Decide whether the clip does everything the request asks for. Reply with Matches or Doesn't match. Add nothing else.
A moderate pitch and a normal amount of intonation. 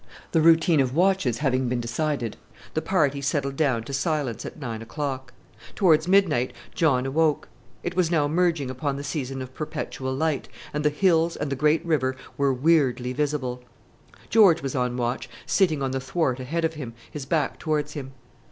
Matches